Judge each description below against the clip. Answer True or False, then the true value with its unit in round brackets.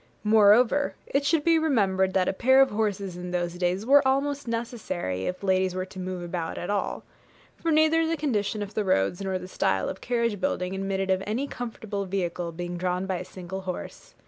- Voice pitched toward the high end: True (195 Hz)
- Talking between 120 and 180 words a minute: False (200 wpm)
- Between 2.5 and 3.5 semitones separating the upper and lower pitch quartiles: False (4.7 semitones)